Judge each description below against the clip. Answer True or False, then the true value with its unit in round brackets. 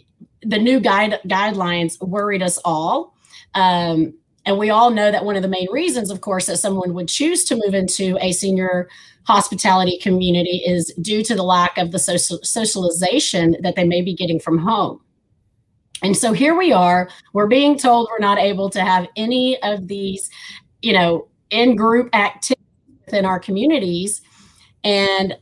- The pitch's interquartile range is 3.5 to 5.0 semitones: False (3.1 semitones)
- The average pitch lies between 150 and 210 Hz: True (190 Hz)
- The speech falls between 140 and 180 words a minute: True (170 wpm)